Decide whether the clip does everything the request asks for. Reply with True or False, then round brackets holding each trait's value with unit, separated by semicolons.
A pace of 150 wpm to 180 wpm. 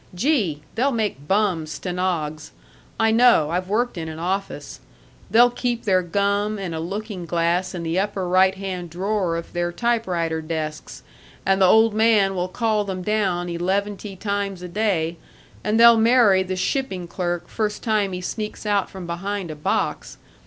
True (165 wpm)